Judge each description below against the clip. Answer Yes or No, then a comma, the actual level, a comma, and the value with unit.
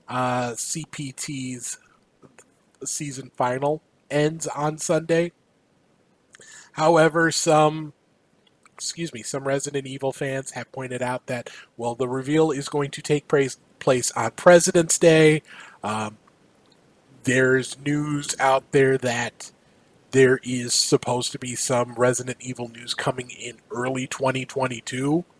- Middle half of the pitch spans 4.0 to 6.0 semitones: No, average, 3.2 semitones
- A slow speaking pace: Yes, slow, 120 wpm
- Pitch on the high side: No, low, 135 Hz